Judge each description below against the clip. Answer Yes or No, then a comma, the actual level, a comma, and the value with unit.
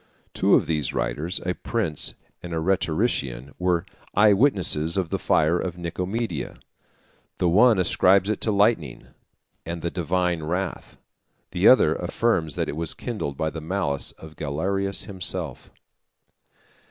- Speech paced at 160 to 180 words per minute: No, average, 140 wpm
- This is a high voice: No, very low, 90 Hz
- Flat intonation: No, average, 3.6 semitones